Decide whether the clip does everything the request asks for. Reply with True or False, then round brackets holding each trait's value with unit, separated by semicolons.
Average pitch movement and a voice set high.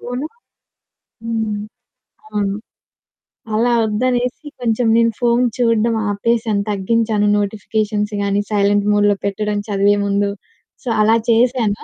False (2.3 semitones; 215 Hz)